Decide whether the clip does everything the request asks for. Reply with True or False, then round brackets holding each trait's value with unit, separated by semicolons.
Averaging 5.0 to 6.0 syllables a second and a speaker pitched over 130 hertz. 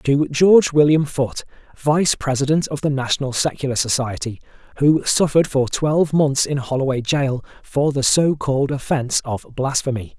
True (5.2 syllables/s; 140 Hz)